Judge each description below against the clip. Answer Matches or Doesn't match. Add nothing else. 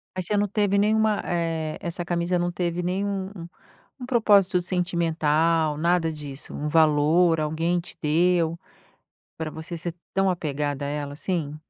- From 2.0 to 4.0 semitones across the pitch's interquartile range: Matches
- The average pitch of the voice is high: Doesn't match